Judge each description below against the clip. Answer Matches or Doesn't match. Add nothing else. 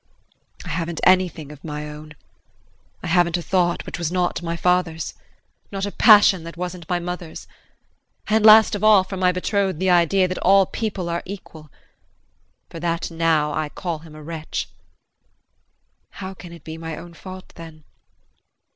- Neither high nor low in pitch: Matches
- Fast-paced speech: Doesn't match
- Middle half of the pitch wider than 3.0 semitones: Doesn't match